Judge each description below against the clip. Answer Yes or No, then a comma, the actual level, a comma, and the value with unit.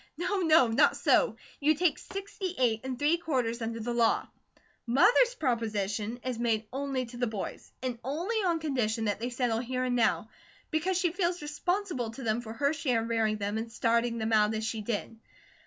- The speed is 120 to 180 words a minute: No, average, 195 wpm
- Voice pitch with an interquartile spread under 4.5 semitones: No, wide, 5.5 semitones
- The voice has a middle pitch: No, high, 245 Hz